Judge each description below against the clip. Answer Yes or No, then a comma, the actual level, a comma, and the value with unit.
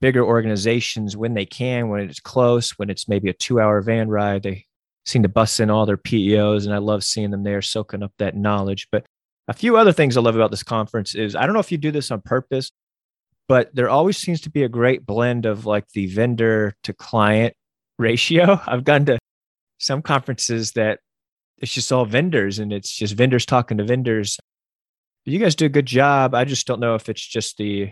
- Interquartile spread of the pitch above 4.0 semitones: No, average, 3.5 semitones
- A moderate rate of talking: No, fast, 220 wpm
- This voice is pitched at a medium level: No, low, 115 Hz